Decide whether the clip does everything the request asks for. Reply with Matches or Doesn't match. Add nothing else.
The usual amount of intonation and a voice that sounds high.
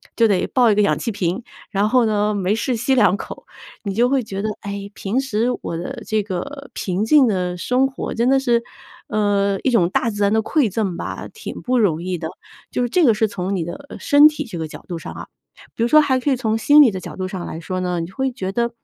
Matches